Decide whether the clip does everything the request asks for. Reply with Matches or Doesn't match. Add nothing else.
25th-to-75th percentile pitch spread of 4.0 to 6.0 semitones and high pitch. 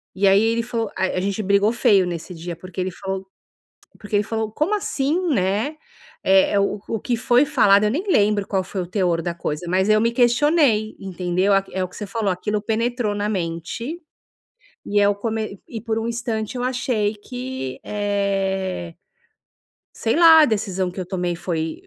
Doesn't match